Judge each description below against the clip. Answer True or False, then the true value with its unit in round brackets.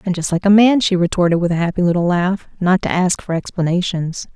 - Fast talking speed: True (235 wpm)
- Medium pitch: True (180 Hz)